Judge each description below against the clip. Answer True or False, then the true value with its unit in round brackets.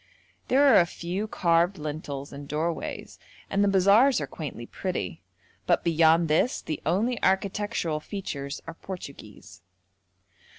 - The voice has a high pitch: False (170 Hz)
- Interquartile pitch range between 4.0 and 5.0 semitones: True (4.6 semitones)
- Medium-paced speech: False (130 wpm)